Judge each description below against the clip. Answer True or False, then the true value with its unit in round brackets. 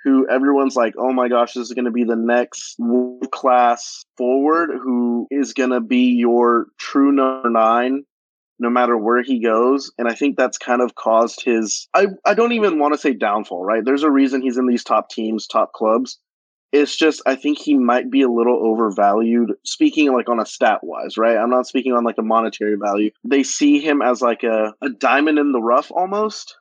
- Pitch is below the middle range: True (125 Hz)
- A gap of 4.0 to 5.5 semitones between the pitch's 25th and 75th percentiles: False (2.9 semitones)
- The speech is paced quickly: True (210 wpm)